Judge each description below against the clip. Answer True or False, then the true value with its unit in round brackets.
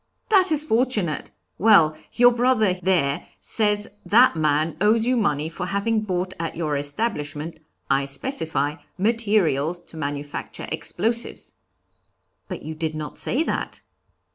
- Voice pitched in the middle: True (180 Hz)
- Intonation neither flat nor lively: False (6.8 semitones)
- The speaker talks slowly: True (130 wpm)